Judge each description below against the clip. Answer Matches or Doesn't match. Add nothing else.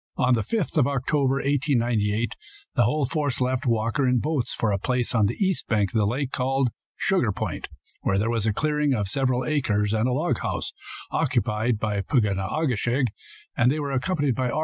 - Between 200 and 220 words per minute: Matches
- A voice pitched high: Doesn't match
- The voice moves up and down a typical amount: Matches